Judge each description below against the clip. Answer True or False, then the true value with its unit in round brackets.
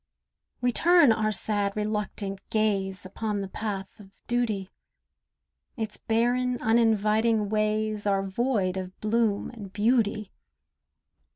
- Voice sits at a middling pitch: False (215 Hz)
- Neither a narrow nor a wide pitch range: False (2.2 semitones)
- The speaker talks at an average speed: False (110 wpm)